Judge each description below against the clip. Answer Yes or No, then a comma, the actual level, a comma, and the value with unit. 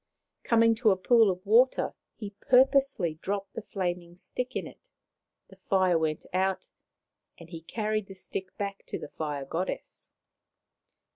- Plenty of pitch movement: No, average, 4.3 semitones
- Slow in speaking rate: No, average, 150 wpm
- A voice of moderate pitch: No, high, 195 Hz